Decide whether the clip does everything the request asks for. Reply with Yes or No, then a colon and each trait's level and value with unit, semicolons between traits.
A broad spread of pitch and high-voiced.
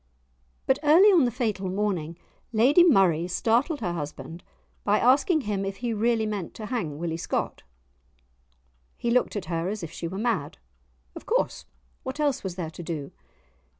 Yes: wide, 6.3 semitones; high, 210 Hz